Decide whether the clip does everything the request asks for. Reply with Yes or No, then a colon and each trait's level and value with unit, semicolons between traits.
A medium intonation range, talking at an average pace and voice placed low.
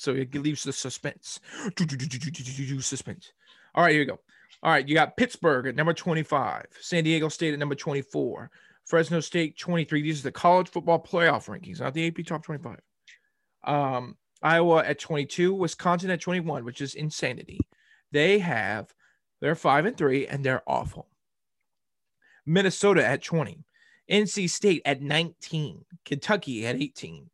No: average, 3.6 semitones; average, 150 wpm; medium, 160 Hz